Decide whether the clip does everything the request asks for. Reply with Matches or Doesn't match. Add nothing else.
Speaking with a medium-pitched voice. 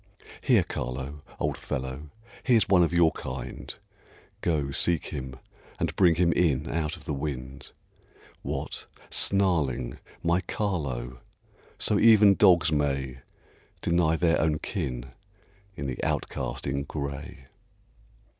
Doesn't match